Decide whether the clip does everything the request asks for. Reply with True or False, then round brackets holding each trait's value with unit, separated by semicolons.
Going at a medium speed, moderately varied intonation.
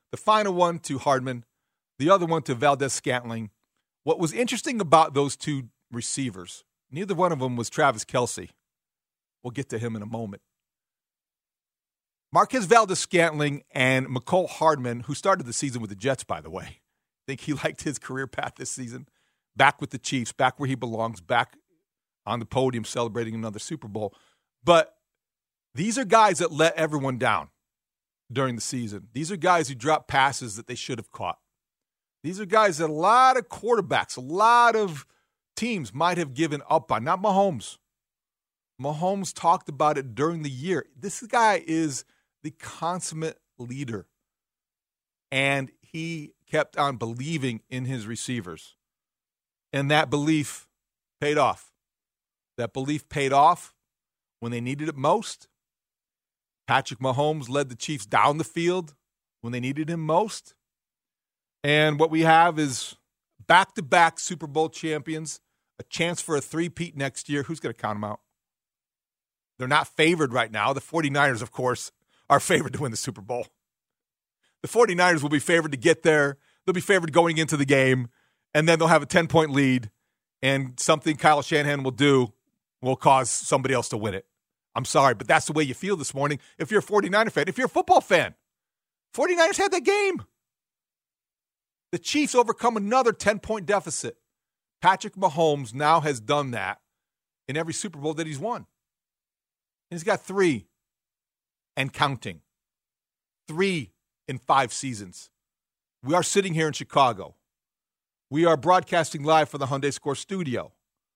True (165 wpm; 4.6 semitones)